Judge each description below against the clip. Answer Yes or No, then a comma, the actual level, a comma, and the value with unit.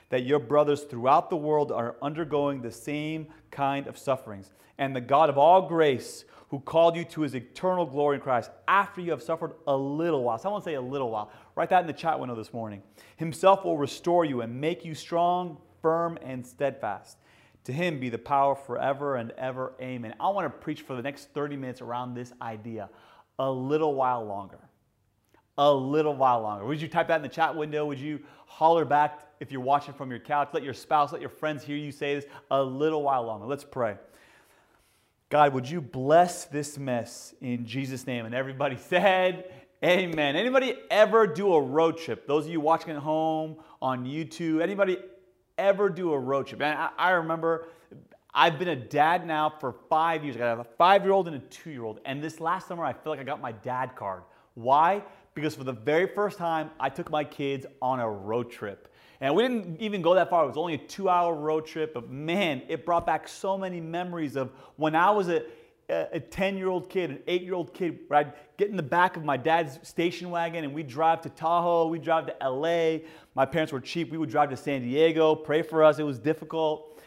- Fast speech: Yes, fast, 215 wpm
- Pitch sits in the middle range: Yes, medium, 150 Hz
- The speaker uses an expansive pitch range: No, average, 3.7 semitones